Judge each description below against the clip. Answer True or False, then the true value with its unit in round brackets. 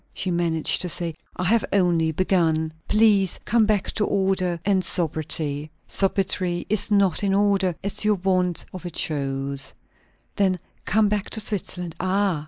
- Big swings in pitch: False (3.3 semitones)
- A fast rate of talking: False (155 wpm)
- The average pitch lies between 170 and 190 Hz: True (185 Hz)